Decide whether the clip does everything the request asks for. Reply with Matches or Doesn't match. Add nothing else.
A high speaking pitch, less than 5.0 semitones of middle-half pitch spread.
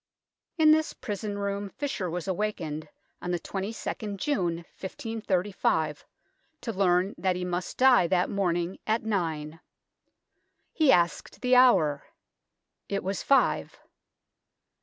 Matches